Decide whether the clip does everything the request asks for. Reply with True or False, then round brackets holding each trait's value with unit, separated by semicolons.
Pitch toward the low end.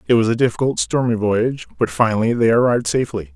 True (115 Hz)